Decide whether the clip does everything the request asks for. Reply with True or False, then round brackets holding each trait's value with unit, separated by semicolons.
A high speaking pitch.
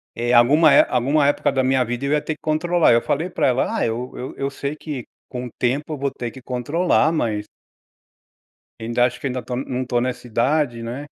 False (130 Hz)